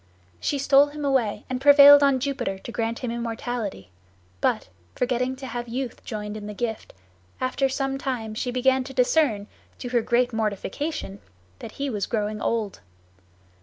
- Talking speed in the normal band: Yes, average, 165 wpm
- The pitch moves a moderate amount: Yes, average, 3.4 semitones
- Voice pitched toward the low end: No, high, 245 Hz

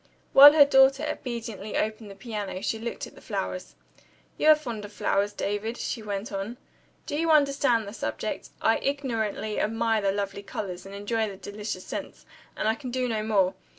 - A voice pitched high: Yes, high, 220 Hz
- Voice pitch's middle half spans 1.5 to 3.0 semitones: No, average, 3.8 semitones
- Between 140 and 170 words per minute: No, average, 185 wpm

